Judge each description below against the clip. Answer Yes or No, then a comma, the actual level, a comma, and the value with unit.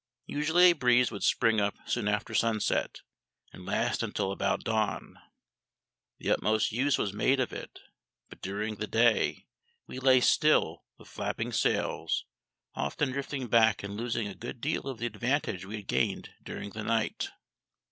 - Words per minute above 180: No, average, 160 wpm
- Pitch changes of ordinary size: Yes, average, 3.7 semitones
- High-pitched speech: No, low, 115 Hz